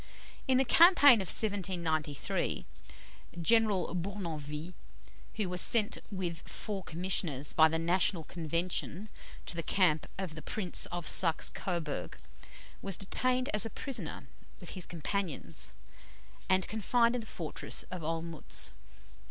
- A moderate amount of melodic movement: Yes, average, 4.1 semitones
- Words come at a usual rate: No, slow, 125 wpm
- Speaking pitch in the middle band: Yes, medium, 180 Hz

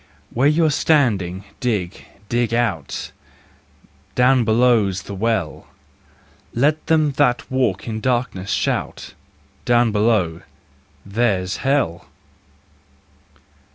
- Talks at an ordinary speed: No, slow, 90 wpm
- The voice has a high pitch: No, low, 115 Hz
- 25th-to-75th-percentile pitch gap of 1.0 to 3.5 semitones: No, average, 4.5 semitones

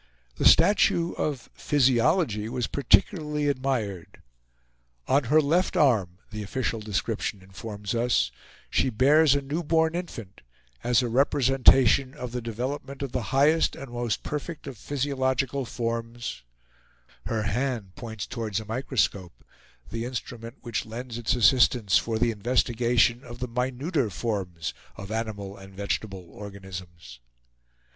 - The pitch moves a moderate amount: Yes, average, 4.2 semitones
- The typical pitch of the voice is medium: No, low, 120 Hz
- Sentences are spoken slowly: Yes, slow, 130 wpm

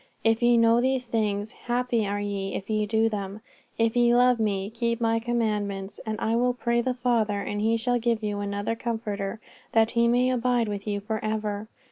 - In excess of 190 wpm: Yes, average, 200 wpm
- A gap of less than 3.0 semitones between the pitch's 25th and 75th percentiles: Yes, narrow, 2.4 semitones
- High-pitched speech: Yes, high, 225 Hz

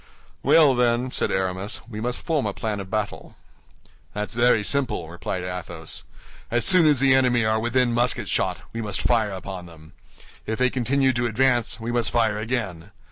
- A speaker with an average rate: Yes, average, 180 wpm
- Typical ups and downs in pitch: Yes, average, 3.7 semitones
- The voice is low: Yes, low, 115 Hz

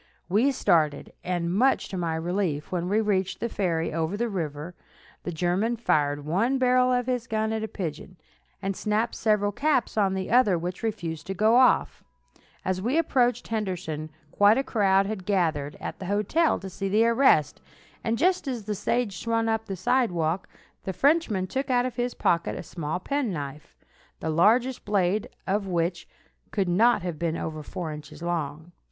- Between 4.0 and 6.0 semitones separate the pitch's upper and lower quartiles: Yes, average, 5.2 semitones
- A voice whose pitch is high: Yes, high, 195 Hz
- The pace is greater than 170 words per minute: Yes, average, 180 wpm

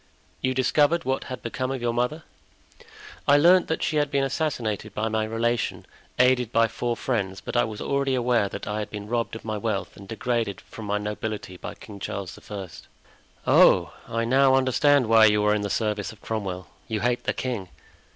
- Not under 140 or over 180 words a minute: No, average, 200 wpm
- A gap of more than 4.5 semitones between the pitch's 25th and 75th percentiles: No, average, 3.6 semitones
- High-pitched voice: No, low, 115 Hz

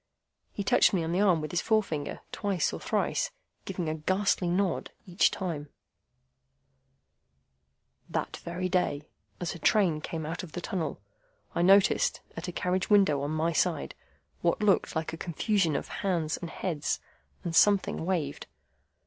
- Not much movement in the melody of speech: No, average, 3.1 semitones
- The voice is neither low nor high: Yes, medium, 175 Hz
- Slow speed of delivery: No, average, 155 wpm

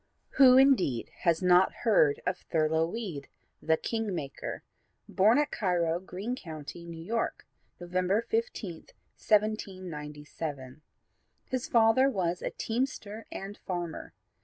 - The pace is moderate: No, slow, 115 wpm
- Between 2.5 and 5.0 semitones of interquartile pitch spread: No, wide, 5.5 semitones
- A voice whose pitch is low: No, medium, 185 Hz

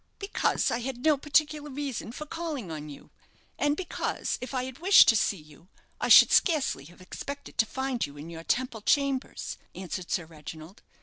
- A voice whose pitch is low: No, very high, 250 Hz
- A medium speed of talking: Yes, average, 185 wpm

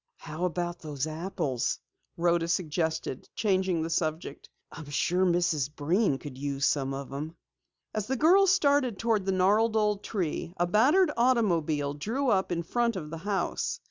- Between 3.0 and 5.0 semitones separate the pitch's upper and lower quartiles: No, wide, 5.6 semitones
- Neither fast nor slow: Yes, average, 160 wpm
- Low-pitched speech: No, medium, 175 Hz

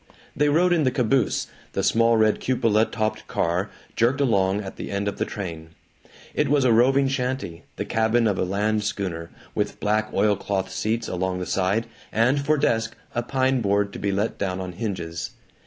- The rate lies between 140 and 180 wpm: No, average, 190 wpm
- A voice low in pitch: Yes, low, 110 Hz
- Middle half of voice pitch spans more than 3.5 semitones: Yes, average, 4.3 semitones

